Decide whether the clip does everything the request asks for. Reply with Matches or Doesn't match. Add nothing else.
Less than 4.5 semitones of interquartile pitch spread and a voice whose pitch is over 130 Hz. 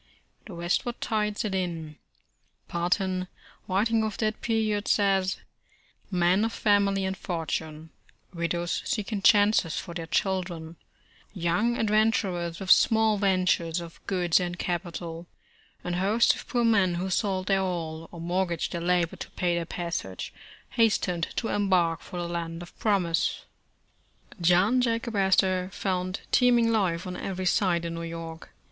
Matches